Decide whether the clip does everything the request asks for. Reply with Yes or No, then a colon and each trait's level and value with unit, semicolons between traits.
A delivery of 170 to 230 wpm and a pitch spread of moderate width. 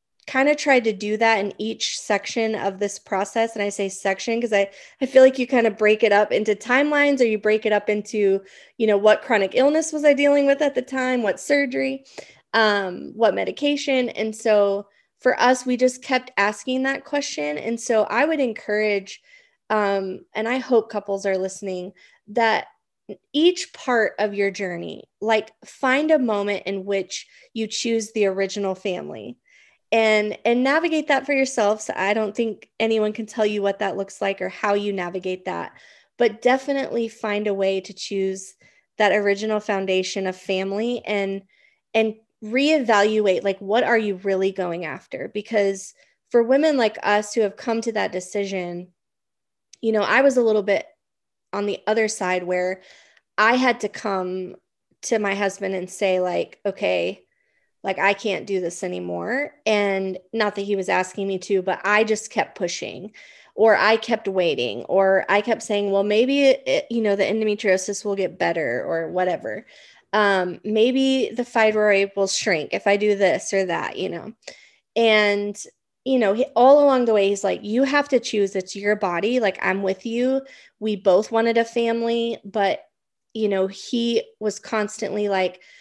Yes: average, 180 wpm; average, 3.2 semitones